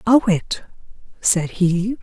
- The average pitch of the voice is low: No, high, 200 Hz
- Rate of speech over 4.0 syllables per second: No, 3.0 syllables/s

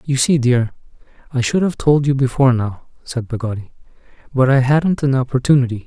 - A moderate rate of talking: Yes, average, 175 wpm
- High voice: No, low, 130 Hz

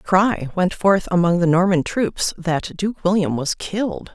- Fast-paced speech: No, average, 190 wpm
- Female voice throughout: Yes, female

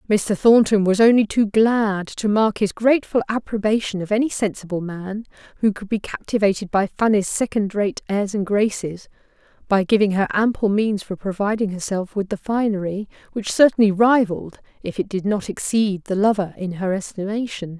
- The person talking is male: No, female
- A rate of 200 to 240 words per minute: No, average, 170 wpm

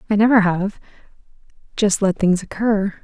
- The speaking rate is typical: No, slow, 120 wpm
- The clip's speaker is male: No, female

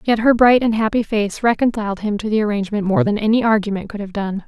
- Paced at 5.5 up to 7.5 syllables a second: Yes, 6.4 syllables/s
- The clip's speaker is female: Yes, female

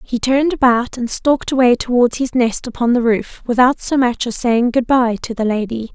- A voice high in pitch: Yes, high, 245 Hz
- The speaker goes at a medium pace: No, fast, 220 wpm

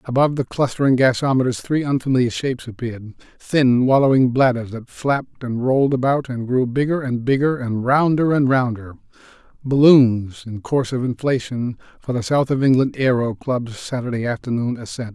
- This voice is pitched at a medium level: No, low, 125 Hz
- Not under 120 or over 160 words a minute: Yes, average, 155 wpm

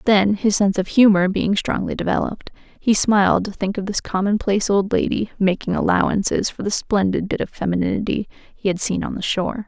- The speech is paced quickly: No, average, 190 wpm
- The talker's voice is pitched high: Yes, high, 200 Hz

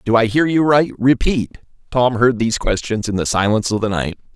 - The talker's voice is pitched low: Yes, low, 120 Hz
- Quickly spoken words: Yes, fast, 220 wpm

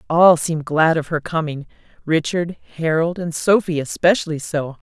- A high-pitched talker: No, medium, 160 Hz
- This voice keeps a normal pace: Yes, average, 150 wpm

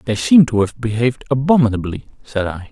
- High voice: No, low, 115 Hz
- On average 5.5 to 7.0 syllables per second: Yes, 5.7 syllables/s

